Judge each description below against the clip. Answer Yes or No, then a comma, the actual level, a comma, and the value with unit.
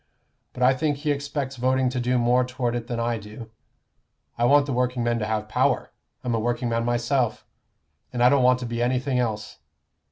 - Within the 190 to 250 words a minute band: Yes, average, 195 wpm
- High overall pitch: No, low, 125 Hz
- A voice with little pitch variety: Yes, narrow, 1.6 semitones